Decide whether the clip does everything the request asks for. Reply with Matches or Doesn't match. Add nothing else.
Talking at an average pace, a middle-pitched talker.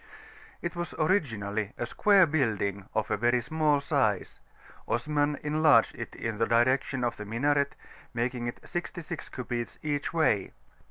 Doesn't match